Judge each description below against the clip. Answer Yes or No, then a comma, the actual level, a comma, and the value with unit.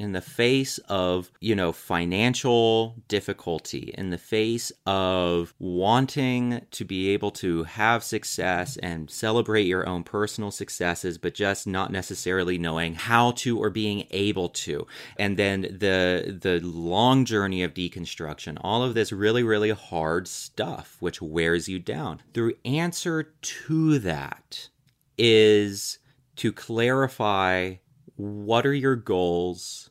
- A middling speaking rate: No, slow, 130 wpm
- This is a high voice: No, low, 100 Hz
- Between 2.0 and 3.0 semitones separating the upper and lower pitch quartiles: No, average, 4.5 semitones